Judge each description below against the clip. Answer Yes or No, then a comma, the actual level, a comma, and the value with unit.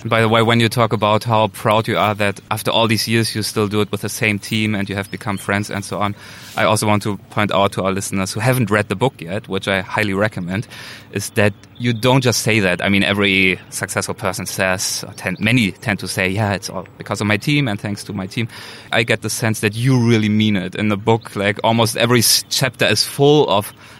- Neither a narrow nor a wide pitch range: No, narrow, 2.2 semitones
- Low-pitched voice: Yes, low, 105 Hz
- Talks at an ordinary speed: No, fast, 255 wpm